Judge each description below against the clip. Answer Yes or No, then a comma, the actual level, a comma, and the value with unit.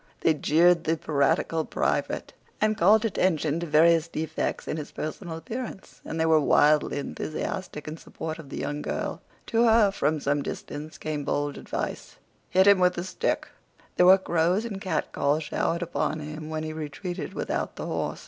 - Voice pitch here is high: No, medium, 160 Hz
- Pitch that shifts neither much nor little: Yes, average, 3.2 semitones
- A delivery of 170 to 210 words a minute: Yes, average, 175 wpm